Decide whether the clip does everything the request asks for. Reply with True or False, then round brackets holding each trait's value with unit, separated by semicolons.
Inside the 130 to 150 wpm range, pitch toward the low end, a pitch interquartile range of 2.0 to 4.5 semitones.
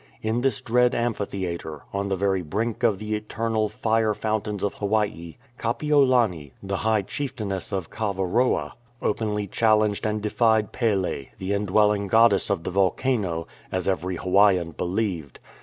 True (140 wpm; 105 Hz; 2.9 semitones)